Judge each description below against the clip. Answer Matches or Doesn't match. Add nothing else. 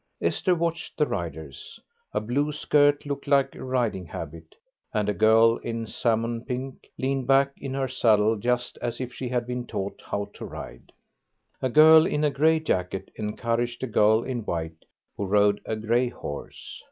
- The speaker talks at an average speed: Matches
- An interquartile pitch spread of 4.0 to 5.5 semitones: Matches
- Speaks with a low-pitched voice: Matches